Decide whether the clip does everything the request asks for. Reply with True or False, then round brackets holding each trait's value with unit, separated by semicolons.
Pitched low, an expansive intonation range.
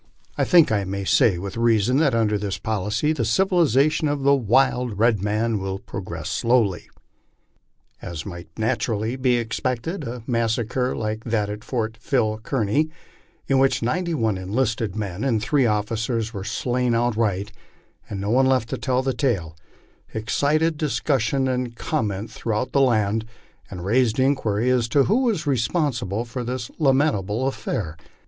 False (115 Hz; 3.9 semitones)